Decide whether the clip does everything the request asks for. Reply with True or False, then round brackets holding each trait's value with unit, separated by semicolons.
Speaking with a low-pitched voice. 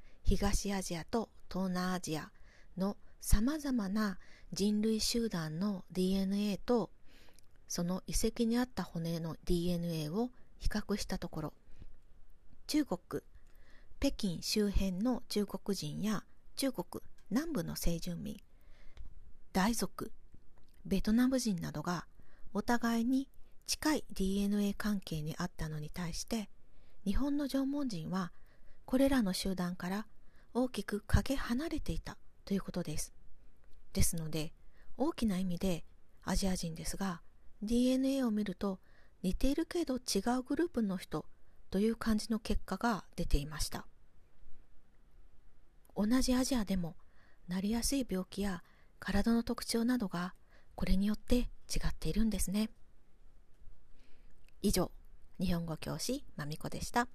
False (195 Hz)